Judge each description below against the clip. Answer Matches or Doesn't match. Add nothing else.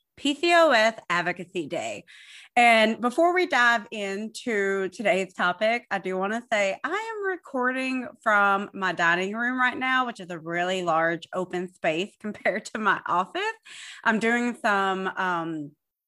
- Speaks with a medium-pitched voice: Doesn't match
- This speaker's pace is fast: Doesn't match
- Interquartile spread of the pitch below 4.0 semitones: Doesn't match